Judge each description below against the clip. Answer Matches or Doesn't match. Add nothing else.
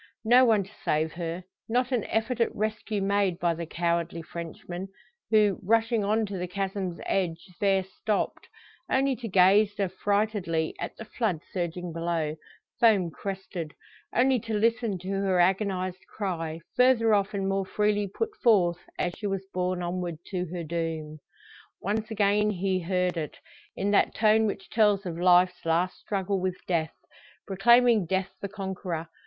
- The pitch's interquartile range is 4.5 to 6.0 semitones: Doesn't match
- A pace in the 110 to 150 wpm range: Doesn't match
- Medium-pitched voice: Doesn't match